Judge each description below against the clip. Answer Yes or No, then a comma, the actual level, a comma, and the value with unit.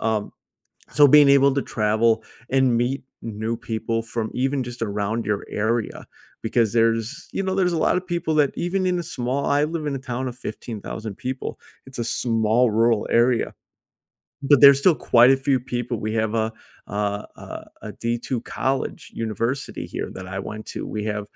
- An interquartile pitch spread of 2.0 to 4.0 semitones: Yes, average, 3.6 semitones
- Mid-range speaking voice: No, low, 120 Hz